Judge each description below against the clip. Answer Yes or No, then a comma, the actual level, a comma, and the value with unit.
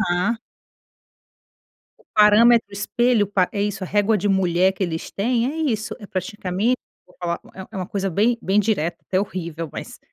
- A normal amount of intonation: Yes, average, 3.1 semitones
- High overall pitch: Yes, high, 200 Hz